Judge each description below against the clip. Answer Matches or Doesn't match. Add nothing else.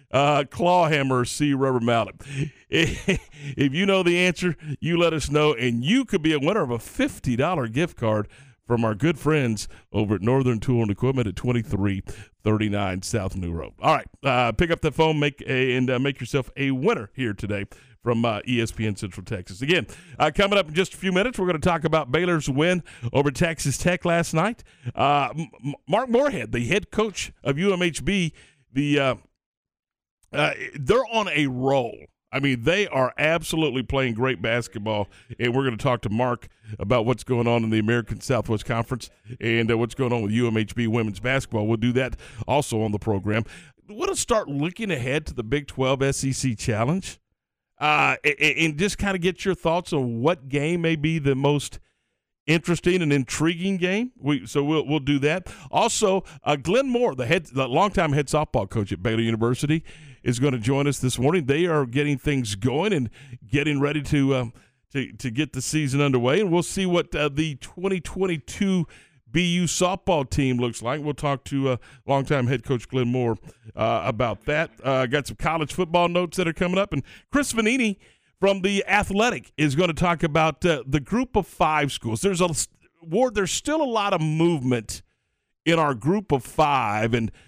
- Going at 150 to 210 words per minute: Matches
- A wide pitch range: Matches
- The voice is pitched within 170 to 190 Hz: Doesn't match